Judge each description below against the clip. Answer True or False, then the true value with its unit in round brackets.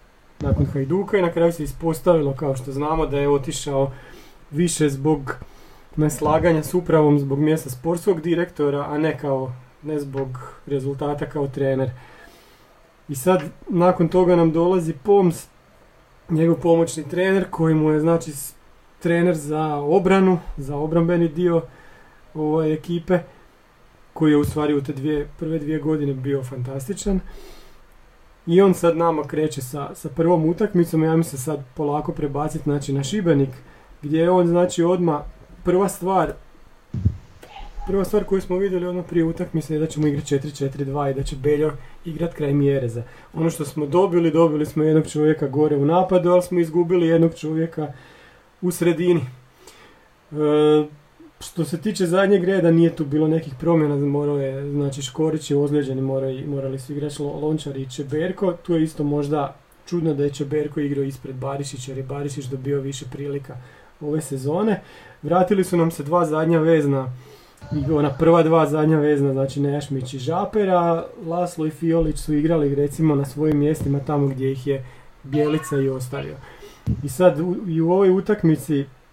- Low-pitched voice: False (155 Hz)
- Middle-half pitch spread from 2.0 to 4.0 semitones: True (2.9 semitones)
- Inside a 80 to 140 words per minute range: False (160 wpm)